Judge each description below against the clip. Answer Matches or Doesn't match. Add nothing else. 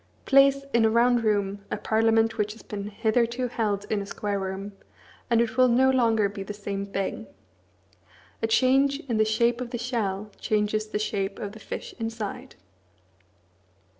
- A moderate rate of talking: Matches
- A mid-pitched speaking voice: Doesn't match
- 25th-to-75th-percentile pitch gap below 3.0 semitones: Matches